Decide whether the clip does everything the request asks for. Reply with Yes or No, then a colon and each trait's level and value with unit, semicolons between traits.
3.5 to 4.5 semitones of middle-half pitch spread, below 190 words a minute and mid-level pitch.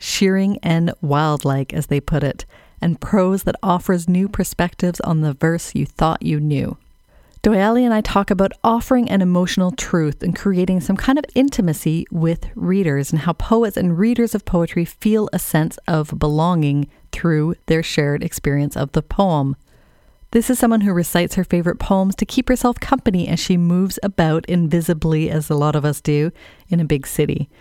Yes: average, 4.0 semitones; average, 180 wpm; medium, 175 Hz